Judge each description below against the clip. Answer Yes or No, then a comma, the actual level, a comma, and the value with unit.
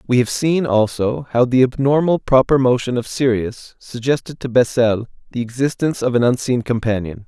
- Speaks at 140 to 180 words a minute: Yes, average, 165 wpm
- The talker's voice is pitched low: Yes, low, 125 Hz